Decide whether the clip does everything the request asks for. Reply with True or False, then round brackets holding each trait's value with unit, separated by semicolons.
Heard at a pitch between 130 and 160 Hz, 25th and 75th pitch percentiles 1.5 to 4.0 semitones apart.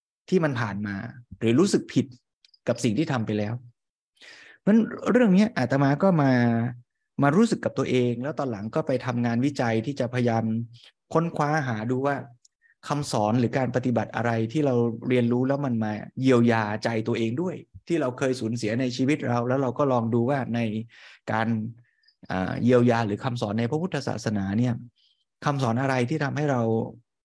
False (120 Hz; 3.3 semitones)